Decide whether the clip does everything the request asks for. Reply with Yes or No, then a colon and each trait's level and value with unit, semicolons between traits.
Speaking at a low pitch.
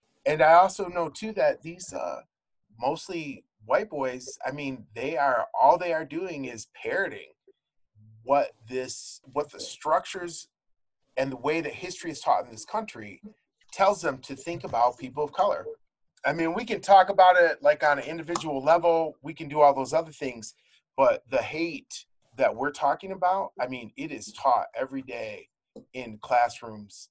No: medium, 160 Hz